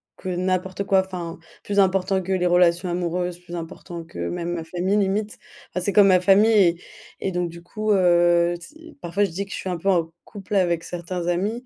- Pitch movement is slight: Yes, narrow, 2.0 semitones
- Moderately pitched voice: Yes, medium, 180 Hz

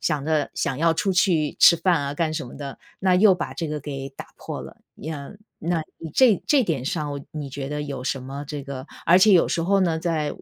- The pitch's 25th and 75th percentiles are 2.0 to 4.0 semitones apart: Yes, average, 3.5 semitones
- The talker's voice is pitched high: No, medium, 155 Hz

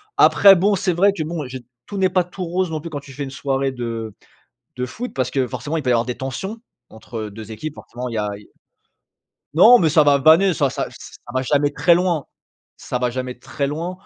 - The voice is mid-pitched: Yes, medium, 145 Hz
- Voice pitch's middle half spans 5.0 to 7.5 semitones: Yes, wide, 5.5 semitones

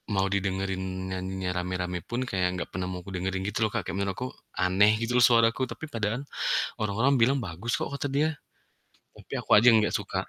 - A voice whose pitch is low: Yes, low, 100 Hz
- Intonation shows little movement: No, average, 3.8 semitones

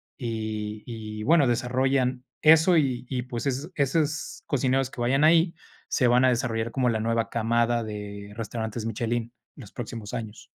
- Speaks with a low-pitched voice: Yes, low, 120 Hz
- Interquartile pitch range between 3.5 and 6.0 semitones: No, average, 3.0 semitones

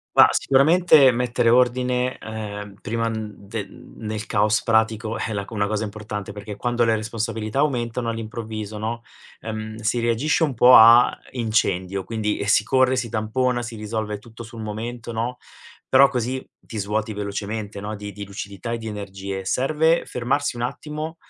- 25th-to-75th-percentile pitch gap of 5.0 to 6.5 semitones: No, narrow, 2.6 semitones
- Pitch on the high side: No, low, 110 Hz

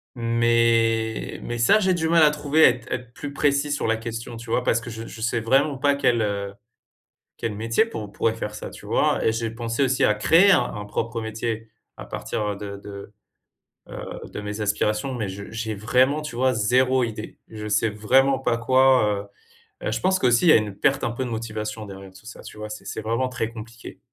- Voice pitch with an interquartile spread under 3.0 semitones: No, average, 3.3 semitones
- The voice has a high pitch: No, low, 115 Hz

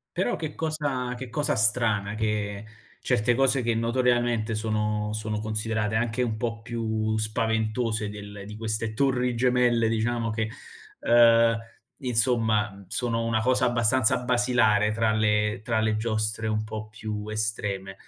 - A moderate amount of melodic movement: No, narrow, 2.0 semitones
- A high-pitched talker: No, low, 110 Hz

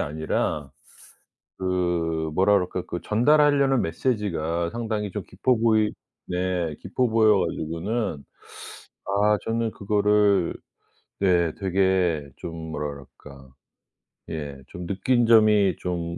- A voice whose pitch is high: No, very low, 95 Hz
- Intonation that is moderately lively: Yes, average, 4.4 semitones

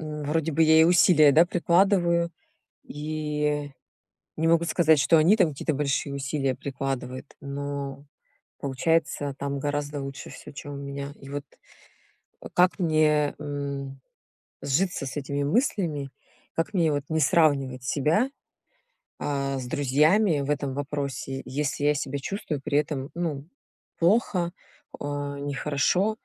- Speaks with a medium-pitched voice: Yes, medium, 145 Hz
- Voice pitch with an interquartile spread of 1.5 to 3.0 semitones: Yes, average, 2.7 semitones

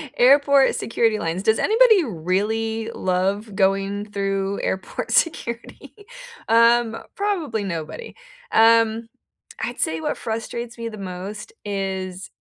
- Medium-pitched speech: No, high, 220 Hz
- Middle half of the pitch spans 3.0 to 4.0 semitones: Yes, average, 3.3 semitones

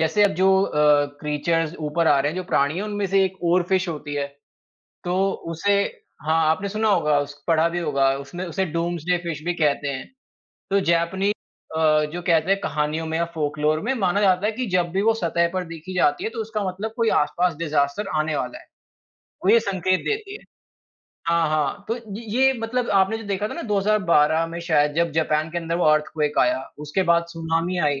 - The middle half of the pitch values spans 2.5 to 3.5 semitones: No, average, 4.2 semitones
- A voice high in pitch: No, medium, 170 Hz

